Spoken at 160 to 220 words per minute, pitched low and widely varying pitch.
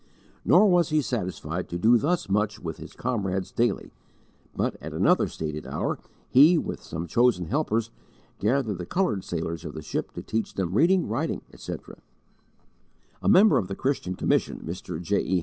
Yes: average, 170 wpm; low, 105 Hz; wide, 7.6 semitones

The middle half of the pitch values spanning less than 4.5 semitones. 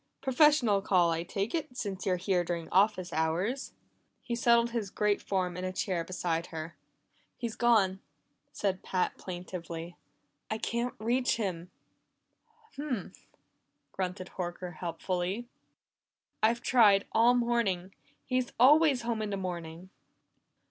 No: average, 4.9 semitones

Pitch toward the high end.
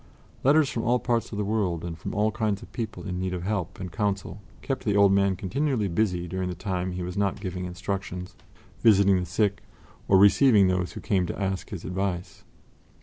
No: very low, 95 Hz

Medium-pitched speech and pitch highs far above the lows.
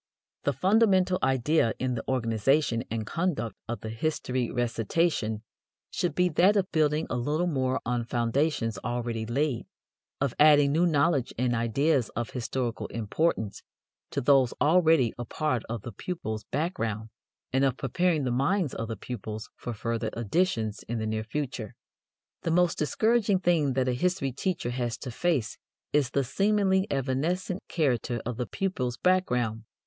No: low, 130 Hz; wide, 5.8 semitones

